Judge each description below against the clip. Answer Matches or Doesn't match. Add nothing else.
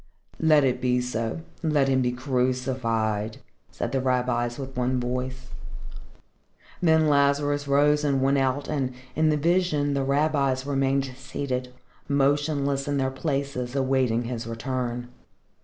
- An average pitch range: Doesn't match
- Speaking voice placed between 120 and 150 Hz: Matches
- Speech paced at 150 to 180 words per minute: Doesn't match